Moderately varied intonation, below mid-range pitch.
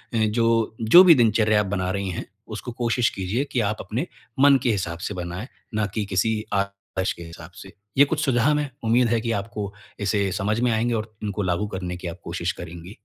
Yes: average, 3.7 semitones; low, 105 Hz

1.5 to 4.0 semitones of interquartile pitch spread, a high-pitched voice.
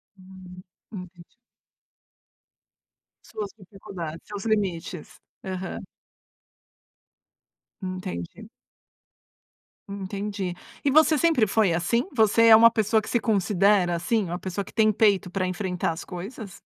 Yes: average, 3.1 semitones; high, 195 Hz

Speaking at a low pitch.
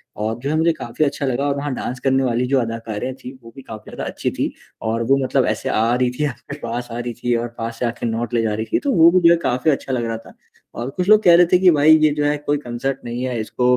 Yes: low, 125 Hz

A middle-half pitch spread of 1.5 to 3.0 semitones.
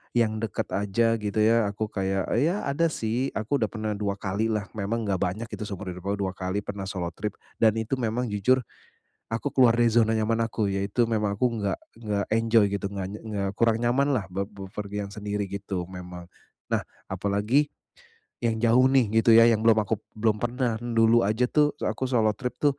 Yes: narrow, 2.6 semitones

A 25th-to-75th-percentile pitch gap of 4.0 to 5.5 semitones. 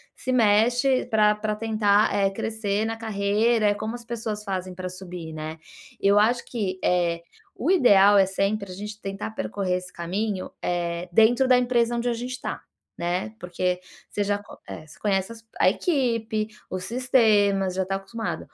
No: average, 3.2 semitones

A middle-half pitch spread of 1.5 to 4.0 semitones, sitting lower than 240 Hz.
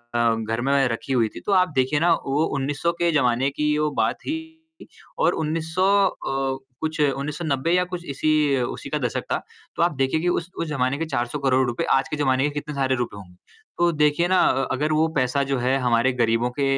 Yes: average, 3.5 semitones; medium, 140 Hz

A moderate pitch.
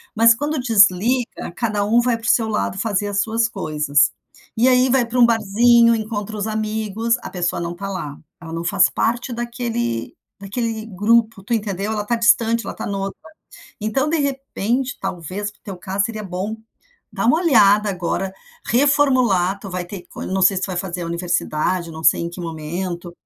No: high, 210 Hz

